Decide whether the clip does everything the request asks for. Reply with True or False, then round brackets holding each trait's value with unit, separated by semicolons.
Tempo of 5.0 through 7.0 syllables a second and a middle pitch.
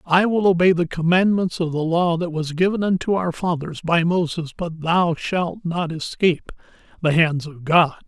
False (4.6 syllables/s; 170 Hz)